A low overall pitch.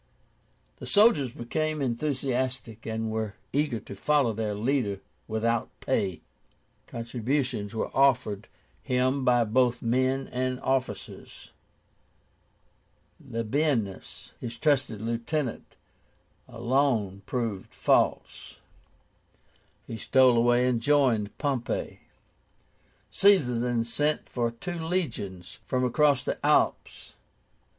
Yes: low, 125 Hz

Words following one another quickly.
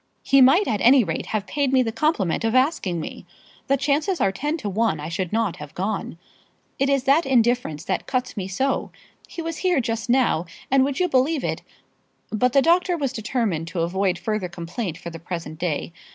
Yes: fast, 210 wpm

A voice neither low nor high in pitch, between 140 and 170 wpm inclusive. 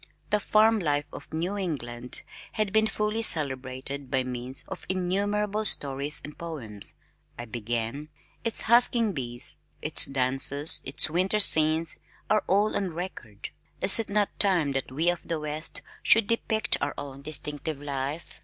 Yes: medium, 155 Hz; average, 150 wpm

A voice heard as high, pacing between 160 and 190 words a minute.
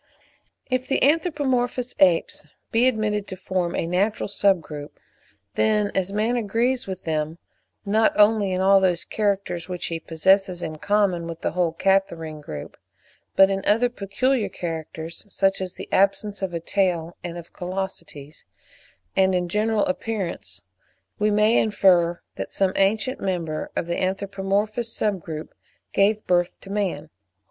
No: high, 195 Hz; average, 150 wpm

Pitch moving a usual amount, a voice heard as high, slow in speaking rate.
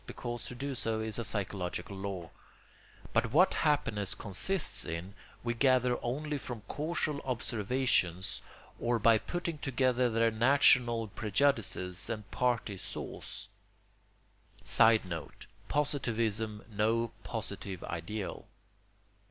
No: average, 3.8 semitones; low, 115 Hz; slow, 105 wpm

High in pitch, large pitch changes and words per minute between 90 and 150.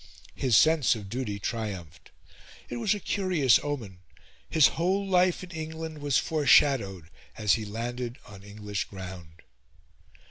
No: low, 120 Hz; wide, 7.7 semitones; slow, 135 wpm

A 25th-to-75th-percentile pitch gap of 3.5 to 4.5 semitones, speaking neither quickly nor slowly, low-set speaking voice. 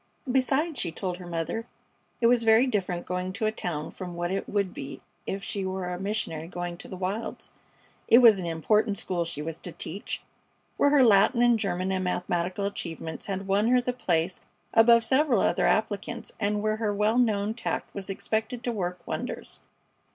No: average, 4.0 semitones; average, 190 wpm; high, 200 Hz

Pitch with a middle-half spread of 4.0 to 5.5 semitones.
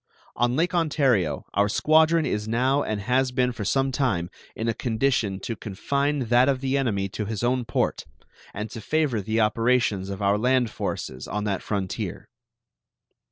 Yes: average, 4.4 semitones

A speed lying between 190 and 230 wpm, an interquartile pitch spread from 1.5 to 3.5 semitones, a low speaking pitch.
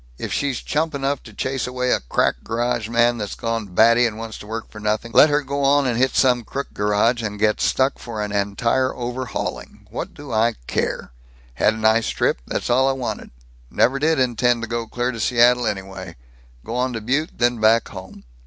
Yes: fast, 205 wpm; average, 2.9 semitones; low, 120 Hz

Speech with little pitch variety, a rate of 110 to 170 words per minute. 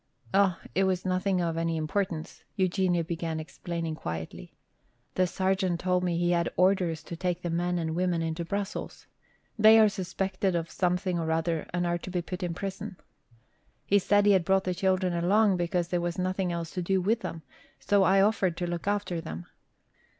No: narrow, 2.1 semitones; average, 190 wpm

